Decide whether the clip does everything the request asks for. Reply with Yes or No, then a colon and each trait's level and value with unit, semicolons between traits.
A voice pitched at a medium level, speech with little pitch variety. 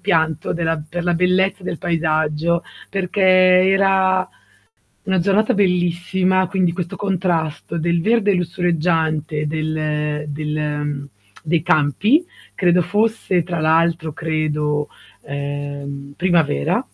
No: medium, 170 Hz; average, 3.3 semitones